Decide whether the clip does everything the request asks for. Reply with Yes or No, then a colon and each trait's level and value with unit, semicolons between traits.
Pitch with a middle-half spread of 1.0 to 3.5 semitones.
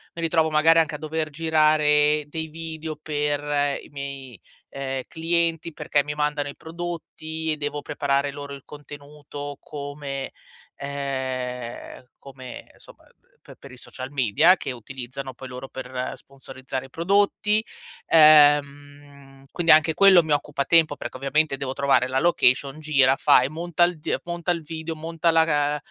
Yes: average, 2.7 semitones